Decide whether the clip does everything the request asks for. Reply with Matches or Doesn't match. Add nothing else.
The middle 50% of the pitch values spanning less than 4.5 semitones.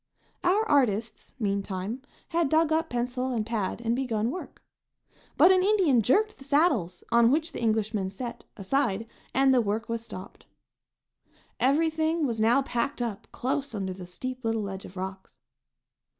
Doesn't match